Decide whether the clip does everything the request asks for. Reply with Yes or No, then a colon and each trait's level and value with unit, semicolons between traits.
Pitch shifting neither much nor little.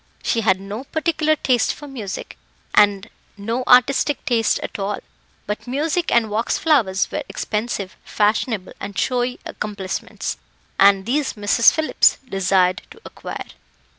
Yes: average, 4.9 semitones